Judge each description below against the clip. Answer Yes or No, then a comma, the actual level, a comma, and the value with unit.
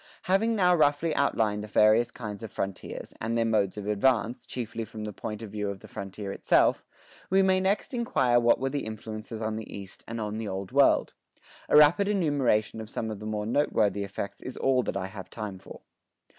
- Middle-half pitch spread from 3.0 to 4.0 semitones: No, average, 4.4 semitones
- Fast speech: Yes, fast, 210 wpm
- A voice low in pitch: Yes, low, 110 Hz